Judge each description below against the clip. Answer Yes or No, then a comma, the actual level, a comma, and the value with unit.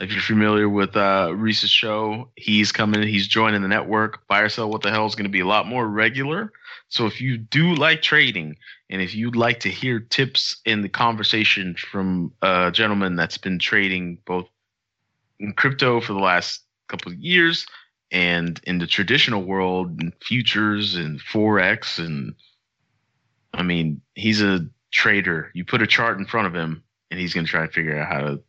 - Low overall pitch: Yes, low, 105 Hz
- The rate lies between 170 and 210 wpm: Yes, average, 190 wpm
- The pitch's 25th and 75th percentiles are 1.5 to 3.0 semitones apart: No, average, 3.7 semitones